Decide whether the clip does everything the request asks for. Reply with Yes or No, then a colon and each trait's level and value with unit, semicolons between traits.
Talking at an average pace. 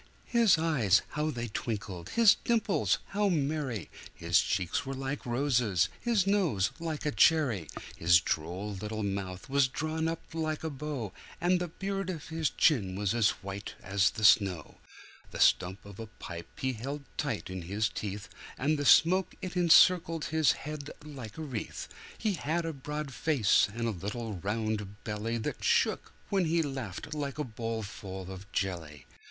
Yes: average, 170 wpm